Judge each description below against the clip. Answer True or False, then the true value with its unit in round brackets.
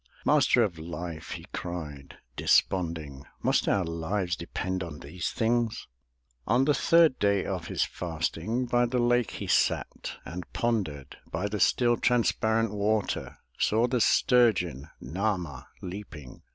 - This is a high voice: False (95 Hz)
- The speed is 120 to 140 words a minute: True (135 wpm)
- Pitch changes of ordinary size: False (5.9 semitones)